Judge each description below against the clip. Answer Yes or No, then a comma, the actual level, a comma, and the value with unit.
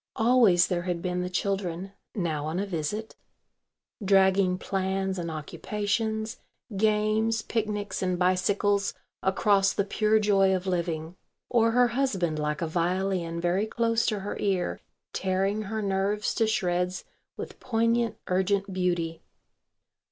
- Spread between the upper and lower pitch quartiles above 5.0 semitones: No, average, 2.9 semitones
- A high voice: Yes, high, 195 Hz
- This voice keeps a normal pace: No, slow, 130 wpm